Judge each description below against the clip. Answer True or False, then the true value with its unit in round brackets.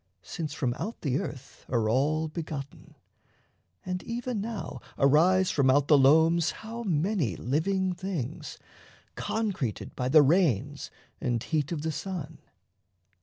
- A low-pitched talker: False (155 Hz)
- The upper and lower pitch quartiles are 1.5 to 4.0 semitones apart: False (5.2 semitones)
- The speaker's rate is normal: False (130 wpm)